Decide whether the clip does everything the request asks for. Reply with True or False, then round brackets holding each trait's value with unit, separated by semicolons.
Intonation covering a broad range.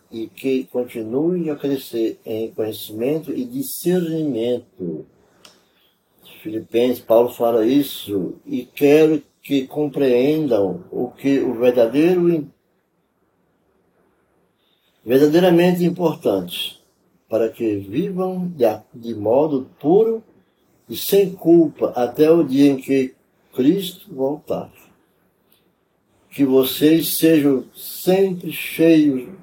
True (5.9 semitones)